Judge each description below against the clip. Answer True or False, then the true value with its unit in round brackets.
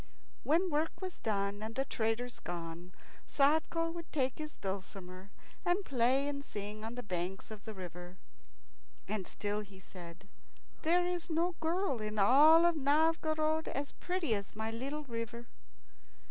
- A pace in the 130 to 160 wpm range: True (145 wpm)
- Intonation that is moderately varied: False (7.7 semitones)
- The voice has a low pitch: False (245 Hz)